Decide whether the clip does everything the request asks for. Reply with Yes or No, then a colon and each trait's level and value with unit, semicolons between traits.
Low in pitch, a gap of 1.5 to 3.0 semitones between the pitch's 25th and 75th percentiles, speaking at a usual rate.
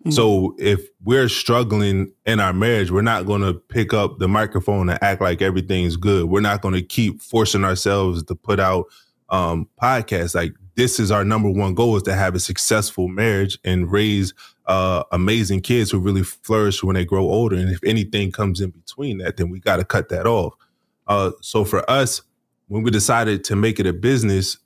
Yes: low, 100 Hz; narrow, 2.6 semitones; average, 195 wpm